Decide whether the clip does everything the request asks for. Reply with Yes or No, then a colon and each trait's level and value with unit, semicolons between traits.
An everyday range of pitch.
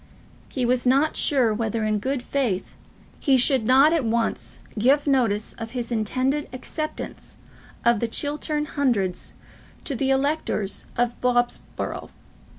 Yes: average, 3.5 semitones